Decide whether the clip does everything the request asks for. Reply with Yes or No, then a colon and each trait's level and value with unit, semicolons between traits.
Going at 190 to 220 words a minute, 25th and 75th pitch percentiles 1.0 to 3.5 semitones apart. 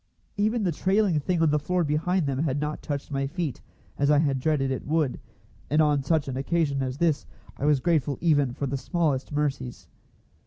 Yes: average, 200 wpm; average, 3.2 semitones